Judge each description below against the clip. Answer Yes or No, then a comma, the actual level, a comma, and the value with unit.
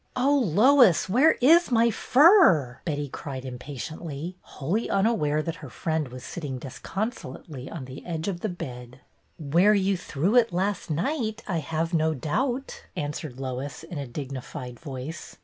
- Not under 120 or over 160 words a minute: No, average, 170 wpm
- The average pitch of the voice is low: No, medium, 160 Hz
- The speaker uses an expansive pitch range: Yes, wide, 7.4 semitones